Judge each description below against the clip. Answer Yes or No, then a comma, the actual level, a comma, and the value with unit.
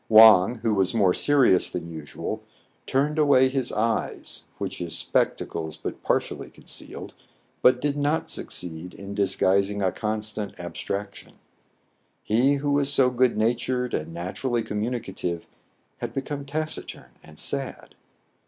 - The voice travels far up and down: Yes, wide, 5.9 semitones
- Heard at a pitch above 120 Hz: No, low, 110 Hz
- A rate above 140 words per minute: No, slow, 135 wpm